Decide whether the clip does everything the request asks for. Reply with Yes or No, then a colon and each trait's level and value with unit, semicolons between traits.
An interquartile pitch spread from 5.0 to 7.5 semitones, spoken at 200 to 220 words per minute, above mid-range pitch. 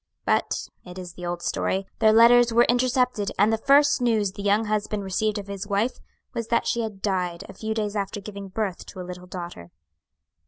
No: average, 3.2 semitones; fast, 205 wpm; high, 205 Hz